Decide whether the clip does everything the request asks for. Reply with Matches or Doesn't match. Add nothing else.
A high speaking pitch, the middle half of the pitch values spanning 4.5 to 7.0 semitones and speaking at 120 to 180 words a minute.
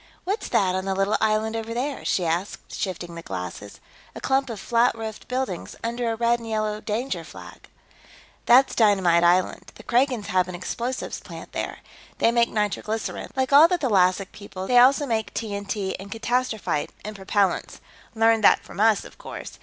Doesn't match